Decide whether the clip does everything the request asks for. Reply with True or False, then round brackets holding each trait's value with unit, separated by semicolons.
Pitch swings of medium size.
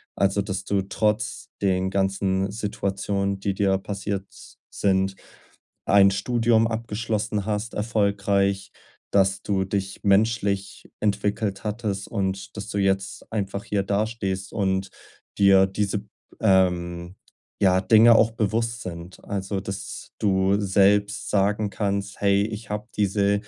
False (1.4 semitones)